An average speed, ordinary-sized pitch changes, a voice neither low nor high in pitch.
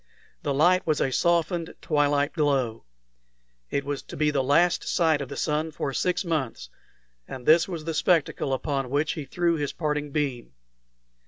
Yes: average, 170 wpm; average, 3.0 semitones; medium, 150 Hz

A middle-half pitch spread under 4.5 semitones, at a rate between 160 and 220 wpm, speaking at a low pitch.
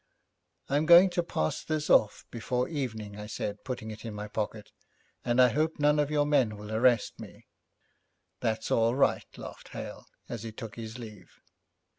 No: average, 5.2 semitones; average, 175 wpm; low, 115 Hz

